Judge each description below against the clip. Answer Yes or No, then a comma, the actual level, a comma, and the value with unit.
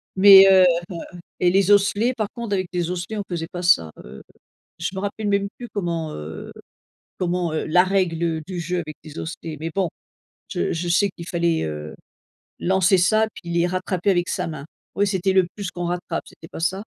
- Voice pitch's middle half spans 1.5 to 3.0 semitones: Yes, narrow, 2.6 semitones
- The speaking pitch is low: No, medium, 180 Hz